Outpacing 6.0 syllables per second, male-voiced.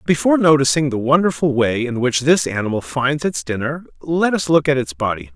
No: 5.5 syllables/s; male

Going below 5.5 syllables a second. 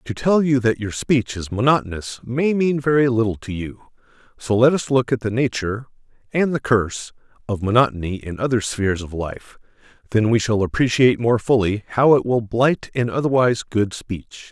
Yes: 5.3 syllables/s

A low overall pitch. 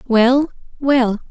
No: very high, 250 Hz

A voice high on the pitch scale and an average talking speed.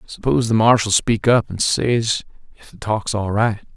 No: low, 110 Hz; average, 190 wpm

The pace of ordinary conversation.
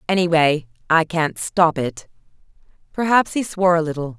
Yes: average, 145 wpm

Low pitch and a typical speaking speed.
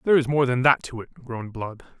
No: low, 125 Hz; fast, 270 wpm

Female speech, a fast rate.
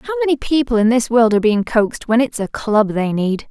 Yes: female; fast, 255 wpm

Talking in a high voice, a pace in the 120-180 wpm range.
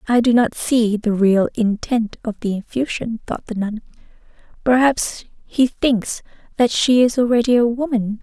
Yes: high, 230 Hz; average, 160 wpm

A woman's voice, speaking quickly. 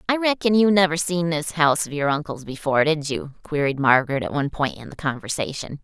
Yes: female; fast, 215 wpm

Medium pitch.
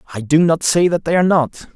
Yes: medium, 160 Hz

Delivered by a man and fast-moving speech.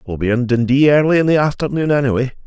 Yes: male; fast, 220 wpm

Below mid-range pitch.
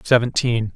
Yes: low, 115 Hz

